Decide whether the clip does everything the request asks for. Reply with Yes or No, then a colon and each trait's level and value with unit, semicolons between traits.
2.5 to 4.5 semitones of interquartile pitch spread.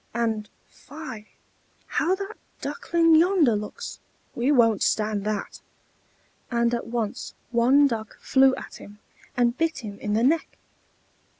No: wide, 5.4 semitones